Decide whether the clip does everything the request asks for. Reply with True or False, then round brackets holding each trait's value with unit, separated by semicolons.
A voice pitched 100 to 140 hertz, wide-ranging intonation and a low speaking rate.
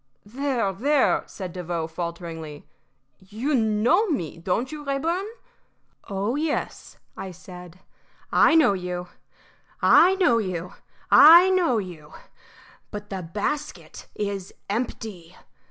False (205 Hz; 7.6 semitones; 110 wpm)